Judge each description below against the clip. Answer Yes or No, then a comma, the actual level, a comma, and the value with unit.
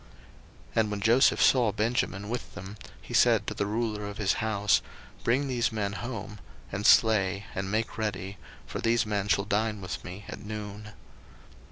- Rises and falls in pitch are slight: Yes, narrow, 1.8 semitones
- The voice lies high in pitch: No, low, 105 Hz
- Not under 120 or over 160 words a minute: No, average, 175 wpm